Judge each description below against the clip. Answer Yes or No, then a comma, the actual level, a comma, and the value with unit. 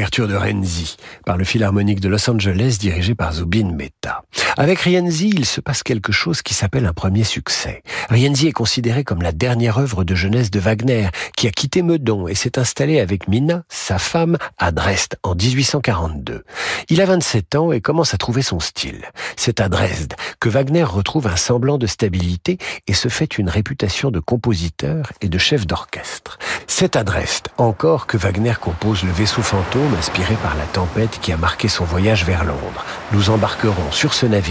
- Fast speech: No, average, 190 wpm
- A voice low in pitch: Yes, low, 110 Hz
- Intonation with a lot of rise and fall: Yes, wide, 5.7 semitones